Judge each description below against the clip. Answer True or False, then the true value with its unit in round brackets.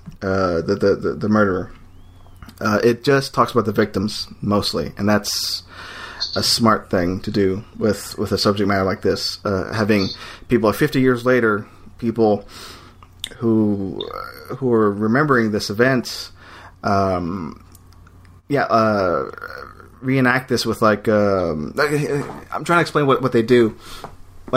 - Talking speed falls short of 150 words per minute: True (140 wpm)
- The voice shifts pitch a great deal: False (3.8 semitones)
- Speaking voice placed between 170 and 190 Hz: False (105 Hz)